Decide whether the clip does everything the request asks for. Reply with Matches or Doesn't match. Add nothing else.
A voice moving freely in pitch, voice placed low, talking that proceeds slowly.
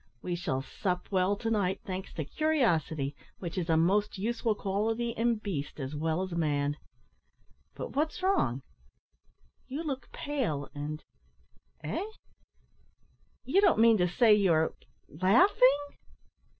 Doesn't match